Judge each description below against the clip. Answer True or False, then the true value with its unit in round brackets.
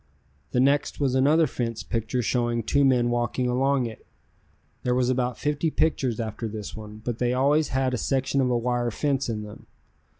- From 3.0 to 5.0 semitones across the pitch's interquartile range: False (2.4 semitones)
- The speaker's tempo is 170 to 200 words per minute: True (190 wpm)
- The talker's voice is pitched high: False (125 Hz)